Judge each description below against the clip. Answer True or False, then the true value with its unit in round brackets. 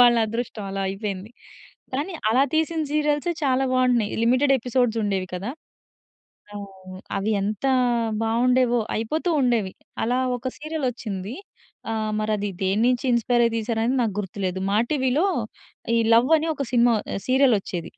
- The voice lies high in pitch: True (235 Hz)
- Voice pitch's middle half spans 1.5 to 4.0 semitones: True (3.5 semitones)